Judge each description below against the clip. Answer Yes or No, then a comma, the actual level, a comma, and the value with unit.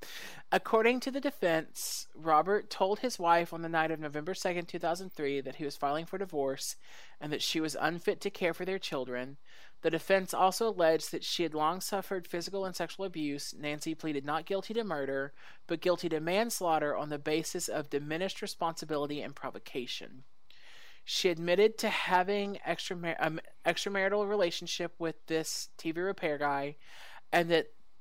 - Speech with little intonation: No, average, 3.9 semitones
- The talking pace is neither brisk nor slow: Yes, average, 165 wpm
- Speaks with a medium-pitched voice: Yes, medium, 170 Hz